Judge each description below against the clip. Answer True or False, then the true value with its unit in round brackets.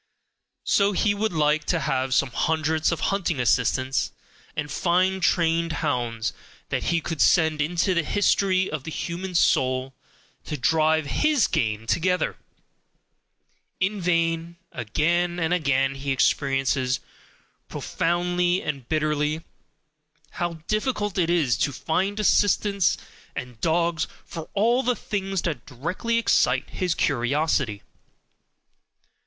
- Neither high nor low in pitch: True (165 Hz)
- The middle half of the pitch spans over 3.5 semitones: True (4.6 semitones)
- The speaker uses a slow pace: True (120 wpm)